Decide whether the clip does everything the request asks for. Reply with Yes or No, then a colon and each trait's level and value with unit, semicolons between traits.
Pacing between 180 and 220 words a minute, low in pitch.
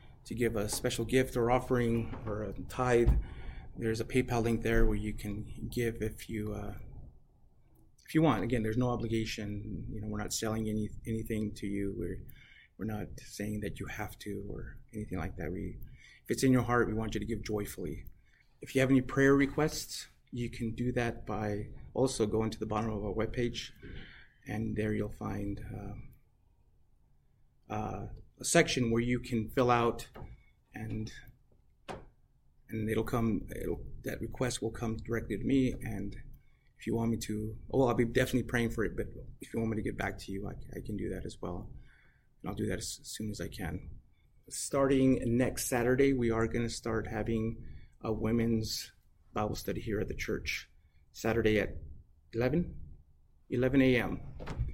Yes: average, 185 wpm; low, 110 Hz